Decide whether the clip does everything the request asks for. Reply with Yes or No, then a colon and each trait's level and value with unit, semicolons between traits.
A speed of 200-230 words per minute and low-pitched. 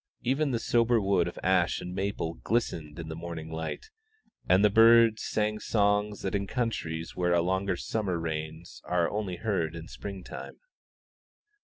No: average, 165 wpm; very low, 95 Hz